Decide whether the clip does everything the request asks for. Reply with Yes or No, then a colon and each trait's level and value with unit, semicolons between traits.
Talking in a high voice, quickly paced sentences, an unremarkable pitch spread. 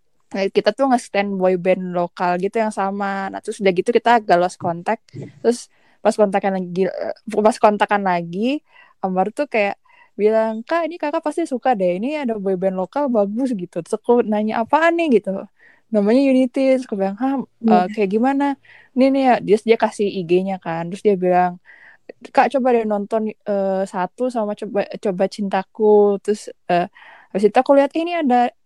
Yes: high, 210 Hz; fast, 190 wpm; average, 4.7 semitones